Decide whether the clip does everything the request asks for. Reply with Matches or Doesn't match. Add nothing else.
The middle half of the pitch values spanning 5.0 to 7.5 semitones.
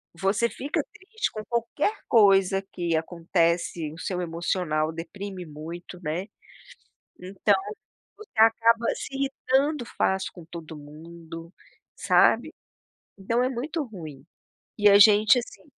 Matches